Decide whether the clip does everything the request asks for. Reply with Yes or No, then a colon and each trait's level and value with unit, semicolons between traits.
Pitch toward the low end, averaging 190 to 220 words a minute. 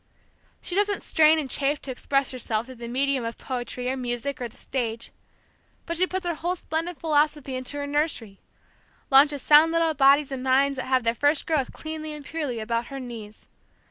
No: very high, 275 Hz; average, 195 wpm